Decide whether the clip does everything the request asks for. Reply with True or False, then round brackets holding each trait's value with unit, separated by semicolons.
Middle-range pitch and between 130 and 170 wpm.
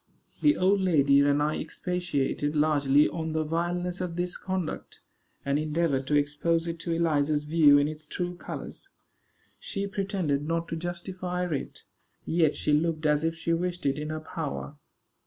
True (160 Hz; 165 wpm)